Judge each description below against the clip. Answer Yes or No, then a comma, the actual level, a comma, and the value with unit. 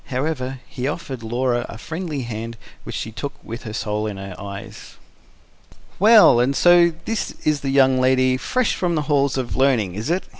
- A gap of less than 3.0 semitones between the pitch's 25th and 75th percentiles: No, average, 4.6 semitones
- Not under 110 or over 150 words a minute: No, average, 185 wpm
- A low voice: Yes, low, 130 Hz